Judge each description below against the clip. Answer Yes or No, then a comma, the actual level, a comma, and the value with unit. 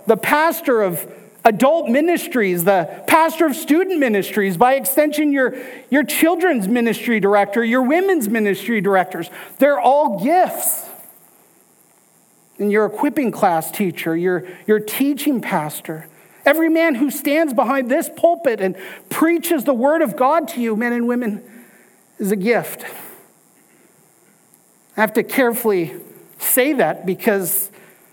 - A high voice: Yes, high, 240 Hz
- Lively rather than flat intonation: Yes, wide, 6.7 semitones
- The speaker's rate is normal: No, slow, 130 wpm